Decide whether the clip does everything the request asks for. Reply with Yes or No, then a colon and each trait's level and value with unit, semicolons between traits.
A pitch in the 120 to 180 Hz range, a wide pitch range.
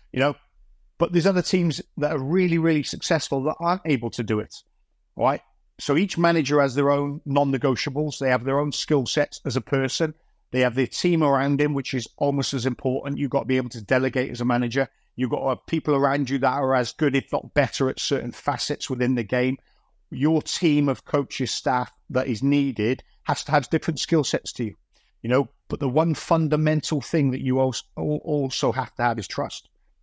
No: medium, 140 Hz; narrow, 2.6 semitones